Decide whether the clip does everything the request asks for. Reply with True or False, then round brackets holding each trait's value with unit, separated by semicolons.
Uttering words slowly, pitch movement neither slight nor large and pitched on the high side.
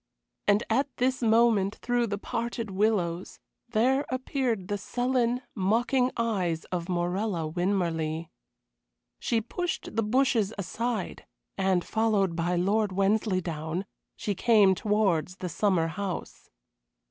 True (115 wpm; 4.3 semitones; 205 Hz)